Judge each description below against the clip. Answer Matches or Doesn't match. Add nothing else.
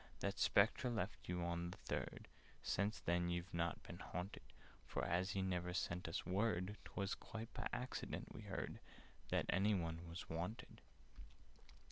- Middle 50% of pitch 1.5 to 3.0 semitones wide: Matches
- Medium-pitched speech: Doesn't match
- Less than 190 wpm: Matches